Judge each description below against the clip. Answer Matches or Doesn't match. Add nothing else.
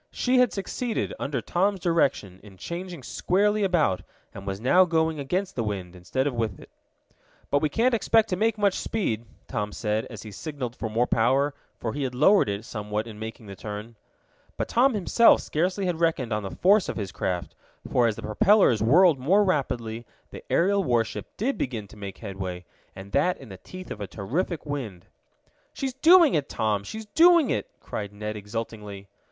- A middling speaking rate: Matches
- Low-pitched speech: Matches